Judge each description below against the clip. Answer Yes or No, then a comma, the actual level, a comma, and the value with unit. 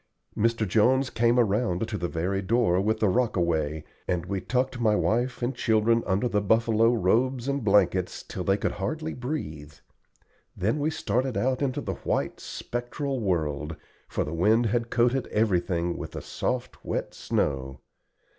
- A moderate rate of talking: Yes, average, 160 wpm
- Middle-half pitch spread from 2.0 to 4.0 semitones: No, average, 5.1 semitones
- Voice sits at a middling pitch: No, low, 110 Hz